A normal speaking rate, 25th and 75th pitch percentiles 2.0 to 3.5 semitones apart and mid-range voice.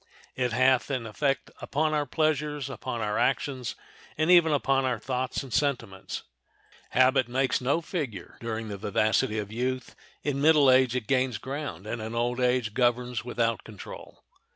No: average, 160 wpm; average, 3.2 semitones; low, 130 Hz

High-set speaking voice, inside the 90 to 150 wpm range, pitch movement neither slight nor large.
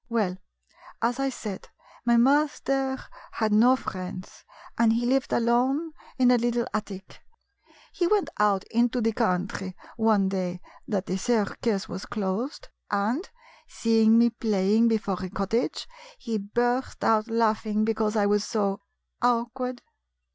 Yes: high, 225 Hz; average, 145 wpm; average, 3.2 semitones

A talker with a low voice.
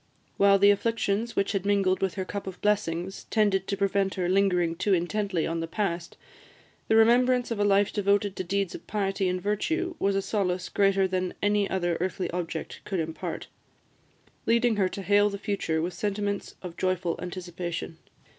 No: high, 195 Hz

